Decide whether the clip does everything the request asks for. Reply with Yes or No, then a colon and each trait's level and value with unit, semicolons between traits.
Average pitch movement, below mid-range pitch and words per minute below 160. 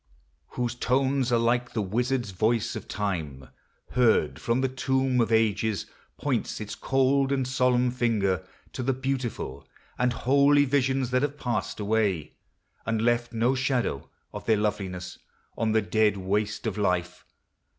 Yes: average, 3.8 semitones; low, 120 Hz; average, 150 wpm